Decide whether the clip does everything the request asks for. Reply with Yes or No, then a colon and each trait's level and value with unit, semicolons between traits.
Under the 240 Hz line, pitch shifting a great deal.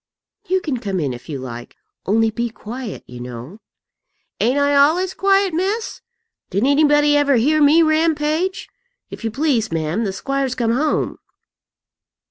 No: very high, 275 Hz; wide, 6.7 semitones